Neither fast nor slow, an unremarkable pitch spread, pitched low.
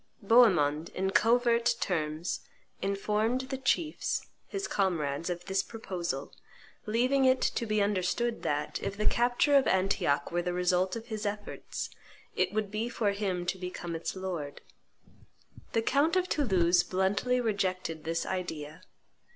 No: average, 145 wpm; average, 4.8 semitones; high, 195 Hz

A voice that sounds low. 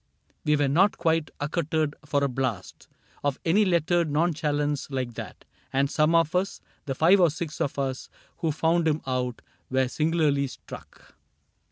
No: medium, 150 Hz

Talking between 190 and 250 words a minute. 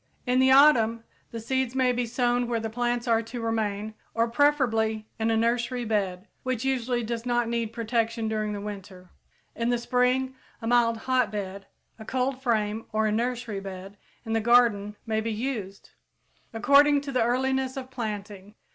No: average, 175 wpm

